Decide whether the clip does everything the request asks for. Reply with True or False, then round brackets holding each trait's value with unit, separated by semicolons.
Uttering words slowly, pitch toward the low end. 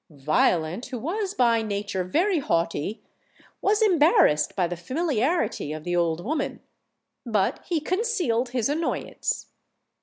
False (125 wpm; 235 Hz)